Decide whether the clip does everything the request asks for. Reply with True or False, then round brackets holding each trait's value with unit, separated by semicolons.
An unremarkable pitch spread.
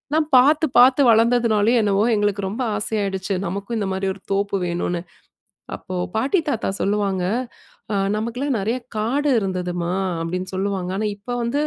True (3.5 semitones)